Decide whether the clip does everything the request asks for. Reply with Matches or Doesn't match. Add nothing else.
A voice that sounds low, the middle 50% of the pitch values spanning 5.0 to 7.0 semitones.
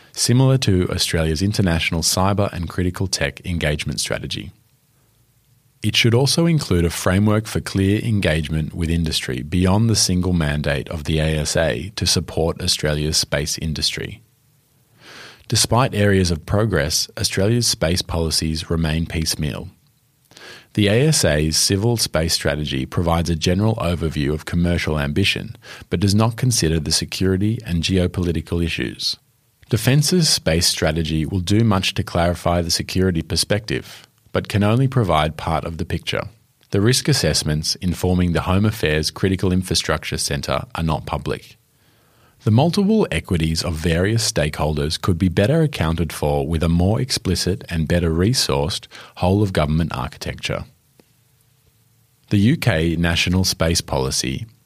Matches